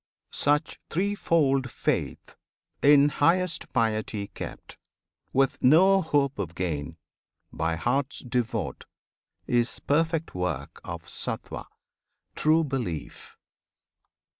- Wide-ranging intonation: Yes, wide, 6.5 semitones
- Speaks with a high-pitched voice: No, low, 135 Hz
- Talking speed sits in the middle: No, slow, 90 wpm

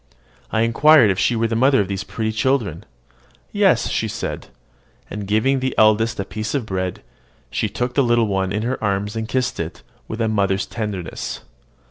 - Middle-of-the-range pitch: No, low, 110 Hz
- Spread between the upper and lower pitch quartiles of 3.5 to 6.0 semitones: No, average, 3.0 semitones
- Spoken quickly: No, average, 185 wpm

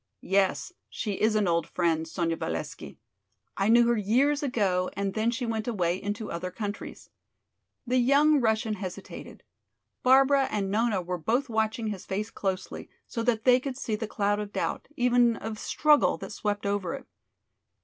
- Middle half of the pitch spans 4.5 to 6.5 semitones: No, average, 3.7 semitones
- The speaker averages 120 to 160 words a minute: No, average, 170 wpm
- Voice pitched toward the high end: Yes, high, 215 Hz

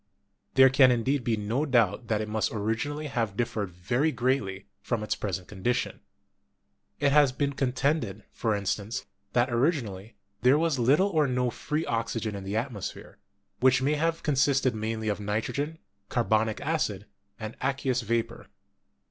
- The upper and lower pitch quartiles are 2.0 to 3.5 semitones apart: No, average, 4.4 semitones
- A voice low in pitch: Yes, low, 120 Hz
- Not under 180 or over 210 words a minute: No, average, 155 wpm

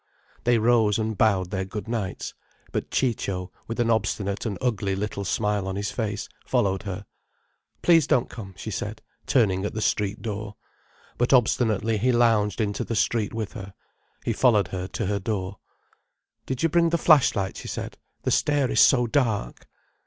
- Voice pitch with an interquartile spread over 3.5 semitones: No, average, 3.2 semitones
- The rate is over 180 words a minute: No, average, 175 wpm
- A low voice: Yes, low, 105 Hz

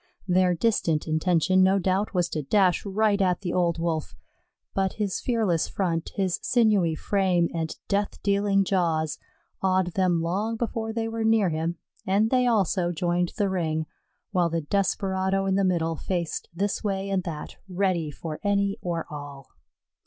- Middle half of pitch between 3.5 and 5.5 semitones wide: No, average, 2.9 semitones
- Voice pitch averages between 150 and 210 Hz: Yes, medium, 185 Hz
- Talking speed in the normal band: Yes, average, 160 wpm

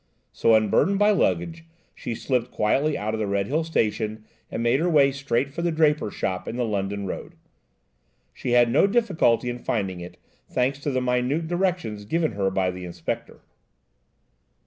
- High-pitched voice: No, low, 125 Hz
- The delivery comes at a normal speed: Yes, average, 170 wpm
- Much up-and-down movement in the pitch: Yes, wide, 6.7 semitones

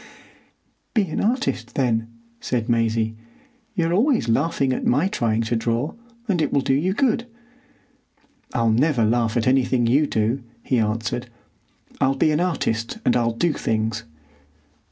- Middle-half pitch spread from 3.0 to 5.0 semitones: No, wide, 5.5 semitones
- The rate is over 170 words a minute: No, average, 150 wpm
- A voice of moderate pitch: No, low, 125 Hz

